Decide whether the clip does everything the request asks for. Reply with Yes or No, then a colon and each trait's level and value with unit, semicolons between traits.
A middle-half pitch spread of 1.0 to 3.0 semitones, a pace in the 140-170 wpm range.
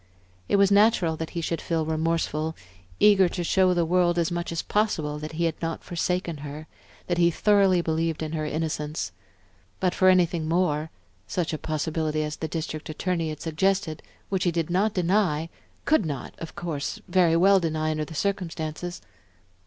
No: narrow, 2.6 semitones; average, 180 wpm